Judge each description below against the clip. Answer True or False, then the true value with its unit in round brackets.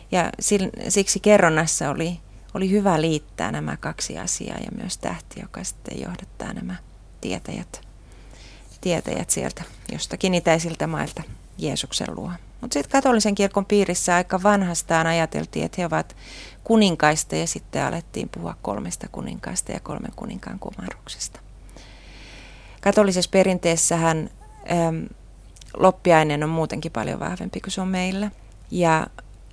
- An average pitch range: True (3.8 semitones)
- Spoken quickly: False (120 wpm)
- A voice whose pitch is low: False (170 Hz)